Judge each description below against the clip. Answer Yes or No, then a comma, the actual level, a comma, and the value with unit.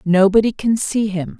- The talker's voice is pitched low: No, high, 205 Hz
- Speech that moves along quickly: No, average, 170 wpm